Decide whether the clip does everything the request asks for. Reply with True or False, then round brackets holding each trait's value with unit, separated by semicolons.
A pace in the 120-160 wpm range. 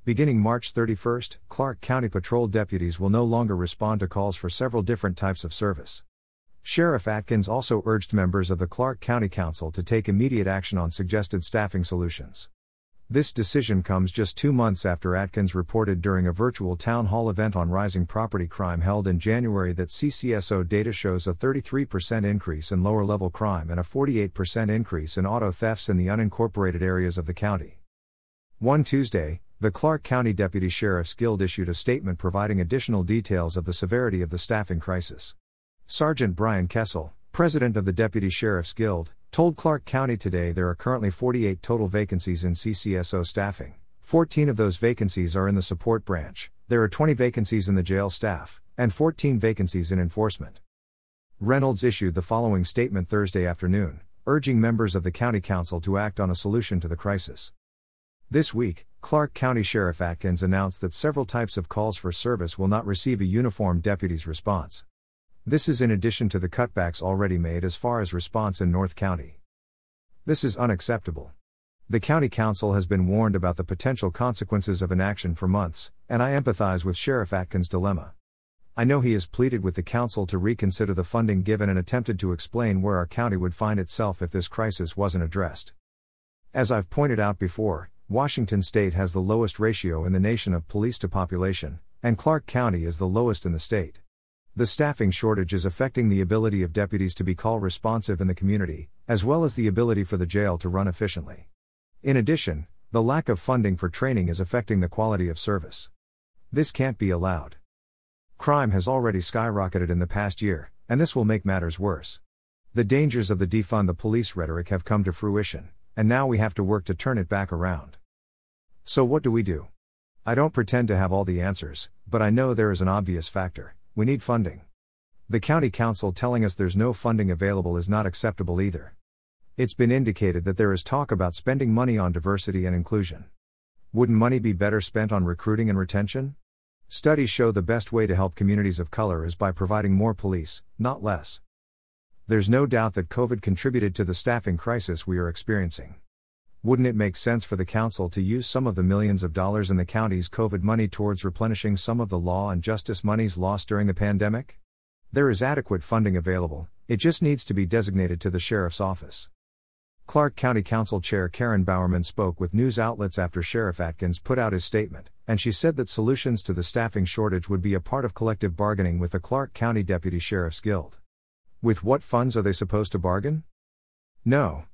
False (190 wpm)